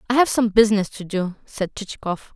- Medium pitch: No, high, 210 Hz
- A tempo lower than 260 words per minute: Yes, fast, 205 wpm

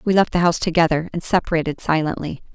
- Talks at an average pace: Yes, average, 190 wpm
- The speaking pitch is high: No, medium, 165 Hz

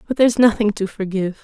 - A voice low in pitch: No, high, 210 Hz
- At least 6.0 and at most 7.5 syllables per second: Yes, 7.1 syllables/s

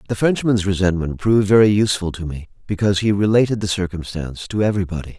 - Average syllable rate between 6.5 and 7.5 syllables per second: Yes, 7.0 syllables/s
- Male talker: Yes, male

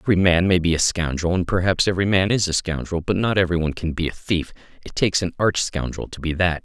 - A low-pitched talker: Yes, very low, 90 Hz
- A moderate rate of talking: No, fast, 260 wpm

